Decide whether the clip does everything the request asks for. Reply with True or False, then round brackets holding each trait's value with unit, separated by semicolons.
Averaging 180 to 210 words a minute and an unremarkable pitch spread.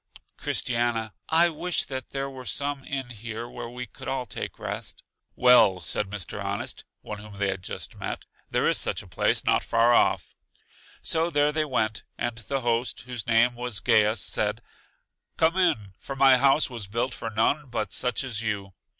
True (185 wpm; 3.9 semitones)